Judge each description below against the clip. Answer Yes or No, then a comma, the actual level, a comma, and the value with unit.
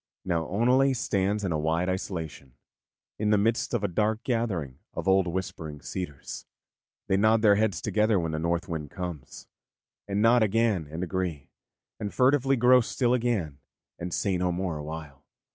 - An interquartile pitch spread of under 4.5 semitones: No, average, 5.1 semitones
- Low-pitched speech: Yes, very low, 95 Hz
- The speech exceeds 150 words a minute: Yes, average, 165 wpm